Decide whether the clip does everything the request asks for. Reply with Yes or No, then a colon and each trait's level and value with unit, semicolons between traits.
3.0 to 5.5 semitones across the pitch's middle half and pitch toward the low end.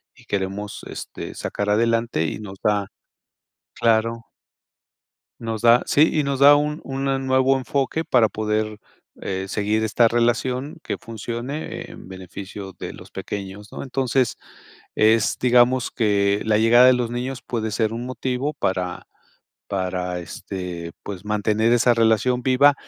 Yes: average, 3.7 semitones; low, 115 Hz